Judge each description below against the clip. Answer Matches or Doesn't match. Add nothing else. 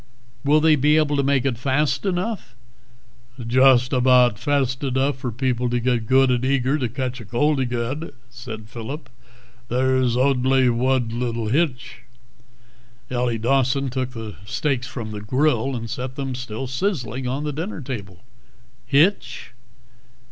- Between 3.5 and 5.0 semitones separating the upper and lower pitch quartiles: Doesn't match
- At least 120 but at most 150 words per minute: Matches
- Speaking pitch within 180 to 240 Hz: Doesn't match